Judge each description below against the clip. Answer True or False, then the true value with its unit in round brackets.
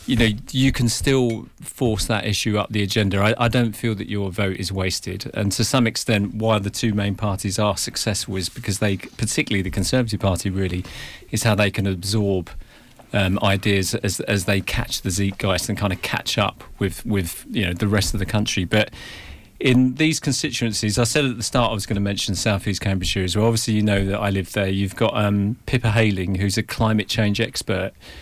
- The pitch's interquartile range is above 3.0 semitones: False (2.6 semitones)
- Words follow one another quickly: True (215 wpm)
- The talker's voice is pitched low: True (105 Hz)